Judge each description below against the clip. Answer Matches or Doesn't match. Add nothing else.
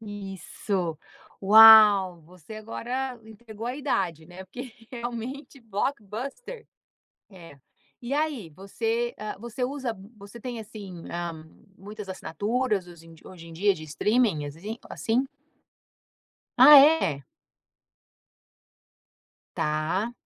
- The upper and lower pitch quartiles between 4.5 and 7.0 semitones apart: Matches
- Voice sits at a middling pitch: Doesn't match